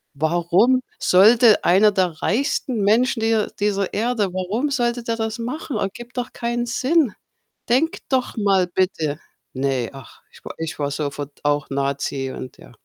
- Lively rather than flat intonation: Yes, wide, 7.0 semitones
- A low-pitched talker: No, high, 205 Hz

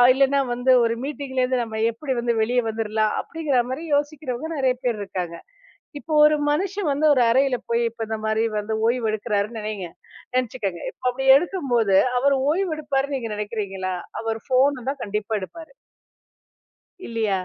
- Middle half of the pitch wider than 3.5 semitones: Yes, average, 4.3 semitones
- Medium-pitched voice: No, high, 245 Hz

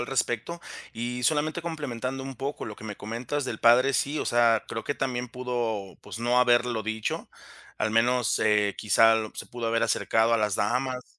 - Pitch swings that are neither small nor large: No, narrow, 2.3 semitones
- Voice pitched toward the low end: Yes, low, 120 Hz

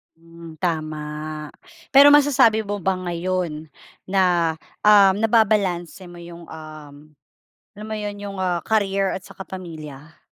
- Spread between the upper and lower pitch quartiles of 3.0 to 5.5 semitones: Yes, average, 3.5 semitones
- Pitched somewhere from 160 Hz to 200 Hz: Yes, medium, 185 Hz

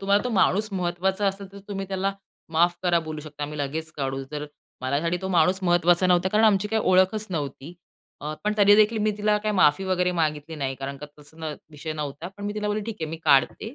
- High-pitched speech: No, medium, 175 Hz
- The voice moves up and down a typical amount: Yes, average, 4.8 semitones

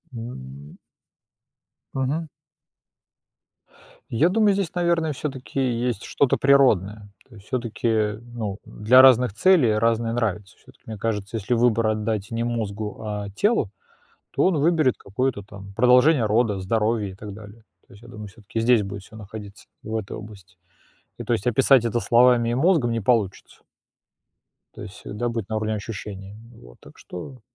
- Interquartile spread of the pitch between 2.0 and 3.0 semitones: No, average, 3.4 semitones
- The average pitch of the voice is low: Yes, low, 115 Hz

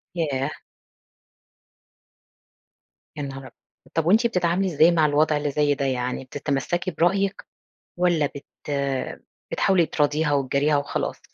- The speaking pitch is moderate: Yes, medium, 150 Hz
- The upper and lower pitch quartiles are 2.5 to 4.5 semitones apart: Yes, average, 3.6 semitones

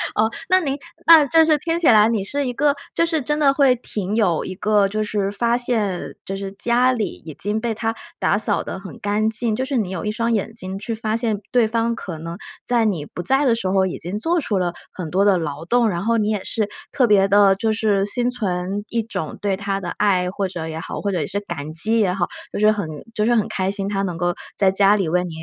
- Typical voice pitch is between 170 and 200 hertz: No, high, 210 Hz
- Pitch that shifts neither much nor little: Yes, average, 3.6 semitones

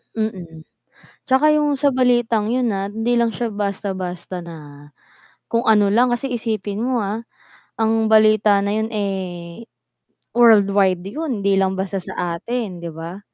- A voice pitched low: No, high, 210 Hz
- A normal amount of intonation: Yes, average, 3.6 semitones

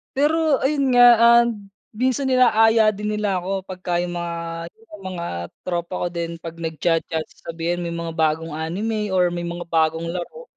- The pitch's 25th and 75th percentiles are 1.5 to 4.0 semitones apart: No, average, 4.8 semitones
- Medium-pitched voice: Yes, medium, 180 Hz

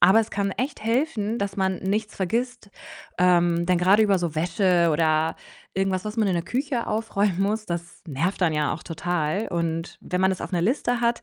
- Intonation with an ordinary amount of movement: Yes, average, 3.9 semitones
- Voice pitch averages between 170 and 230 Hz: Yes, high, 190 Hz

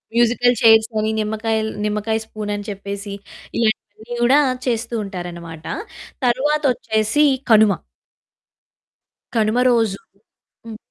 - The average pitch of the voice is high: Yes, high, 220 Hz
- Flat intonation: Yes, narrow, 2.2 semitones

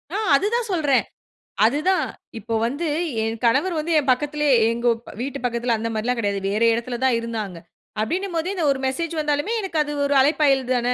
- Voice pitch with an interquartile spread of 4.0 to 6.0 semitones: Yes, average, 5.2 semitones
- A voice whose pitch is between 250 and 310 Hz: Yes, very high, 270 Hz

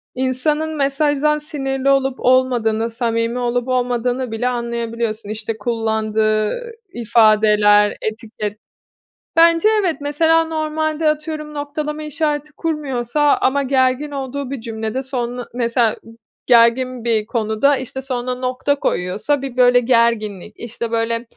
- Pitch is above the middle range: Yes, very high, 250 Hz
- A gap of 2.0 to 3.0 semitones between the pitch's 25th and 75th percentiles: No, average, 3.9 semitones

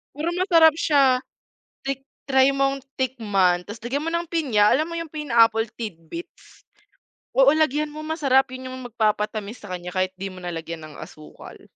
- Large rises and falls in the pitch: Yes, wide, 6.4 semitones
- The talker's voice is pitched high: Yes, very high, 255 Hz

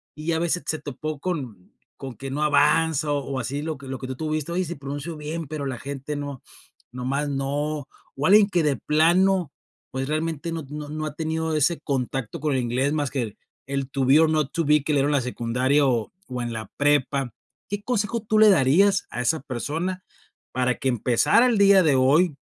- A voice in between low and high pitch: Yes, medium, 145 Hz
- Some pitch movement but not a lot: Yes, average, 3.4 semitones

